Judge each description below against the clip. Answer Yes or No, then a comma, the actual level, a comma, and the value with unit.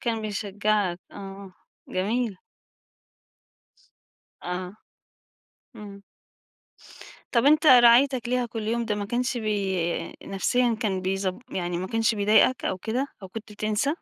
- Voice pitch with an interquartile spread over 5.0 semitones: No, average, 3.6 semitones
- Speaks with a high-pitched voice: Yes, high, 215 Hz